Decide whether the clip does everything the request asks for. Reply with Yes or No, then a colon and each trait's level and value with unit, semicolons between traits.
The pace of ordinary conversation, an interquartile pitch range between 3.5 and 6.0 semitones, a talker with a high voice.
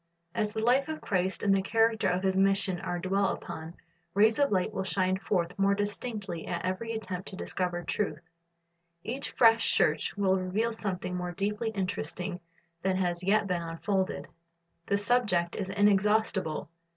No: average, 165 wpm; average, 2.8 semitones; high, 195 Hz